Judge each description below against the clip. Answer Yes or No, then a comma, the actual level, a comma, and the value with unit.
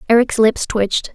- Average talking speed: Yes, average, 155 wpm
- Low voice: No, high, 225 Hz